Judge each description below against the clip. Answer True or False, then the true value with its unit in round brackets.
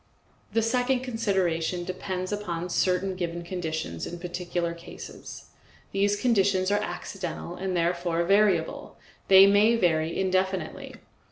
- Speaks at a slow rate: True (115 wpm)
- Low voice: False (185 Hz)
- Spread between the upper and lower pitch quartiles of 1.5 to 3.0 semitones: True (2.7 semitones)